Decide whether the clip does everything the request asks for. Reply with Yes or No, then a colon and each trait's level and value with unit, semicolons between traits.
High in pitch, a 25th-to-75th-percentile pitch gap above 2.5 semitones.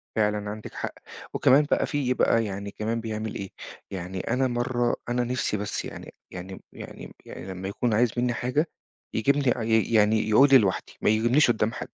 No: low, 110 Hz; average, 2.9 semitones